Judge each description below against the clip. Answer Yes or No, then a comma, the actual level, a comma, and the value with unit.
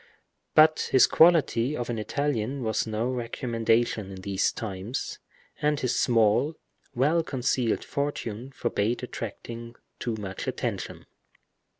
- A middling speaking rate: No, slow, 115 wpm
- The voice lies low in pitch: Yes, low, 120 Hz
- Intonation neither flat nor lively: Yes, average, 3.7 semitones